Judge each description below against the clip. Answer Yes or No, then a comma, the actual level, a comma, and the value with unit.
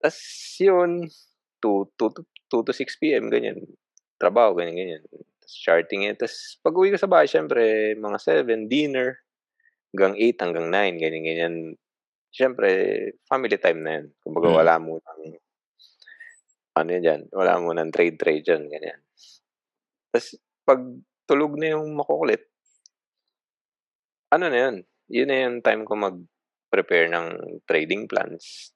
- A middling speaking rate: Yes, average, 140 wpm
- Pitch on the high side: No, low, 135 Hz